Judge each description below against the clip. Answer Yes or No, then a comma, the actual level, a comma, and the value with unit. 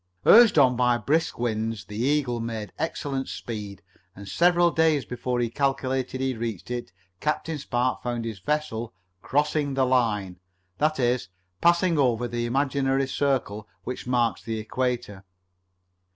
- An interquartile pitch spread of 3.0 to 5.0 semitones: Yes, average, 3.6 semitones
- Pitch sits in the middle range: No, low, 125 Hz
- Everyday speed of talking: Yes, average, 145 wpm